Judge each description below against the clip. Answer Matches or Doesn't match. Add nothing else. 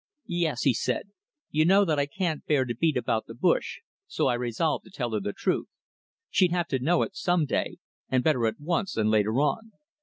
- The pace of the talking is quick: Matches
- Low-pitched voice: Doesn't match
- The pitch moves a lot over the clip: Matches